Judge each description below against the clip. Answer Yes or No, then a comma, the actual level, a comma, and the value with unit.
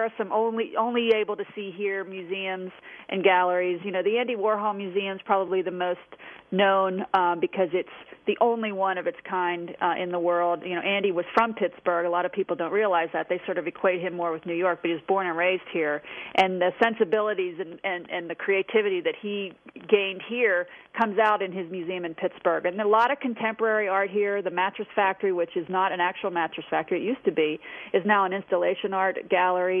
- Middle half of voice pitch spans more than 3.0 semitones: No, narrow, 2.5 semitones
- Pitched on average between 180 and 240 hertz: Yes, high, 190 Hz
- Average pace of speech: No, fast, 220 wpm